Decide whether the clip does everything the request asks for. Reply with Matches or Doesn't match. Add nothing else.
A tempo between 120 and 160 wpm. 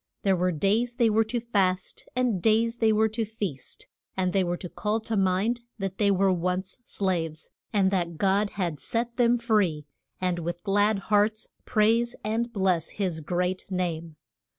Doesn't match